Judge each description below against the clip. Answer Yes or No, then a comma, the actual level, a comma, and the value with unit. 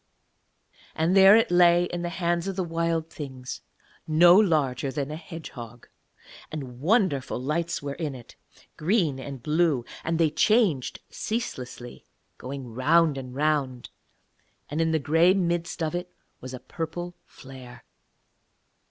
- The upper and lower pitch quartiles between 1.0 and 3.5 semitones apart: No, average, 4.5 semitones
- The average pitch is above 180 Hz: No, medium, 160 Hz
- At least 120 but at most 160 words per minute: Yes, average, 140 wpm